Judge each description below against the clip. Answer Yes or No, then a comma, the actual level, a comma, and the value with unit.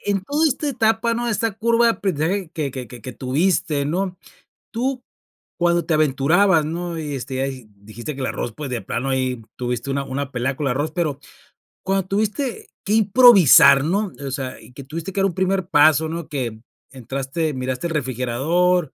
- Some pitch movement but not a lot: No, wide, 6.5 semitones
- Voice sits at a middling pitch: Yes, medium, 155 Hz